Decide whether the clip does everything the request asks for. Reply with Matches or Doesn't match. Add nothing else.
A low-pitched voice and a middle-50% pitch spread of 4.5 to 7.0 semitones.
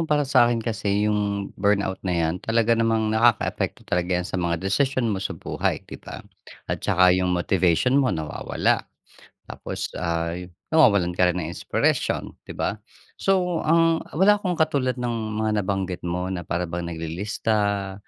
Matches